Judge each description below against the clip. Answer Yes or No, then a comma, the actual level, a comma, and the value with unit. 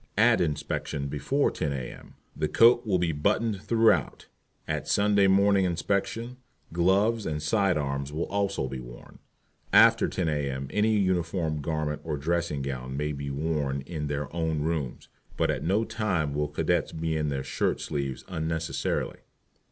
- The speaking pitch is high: No, very low, 80 Hz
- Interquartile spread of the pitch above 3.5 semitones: Yes, average, 5.1 semitones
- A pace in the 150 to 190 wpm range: Yes, average, 155 wpm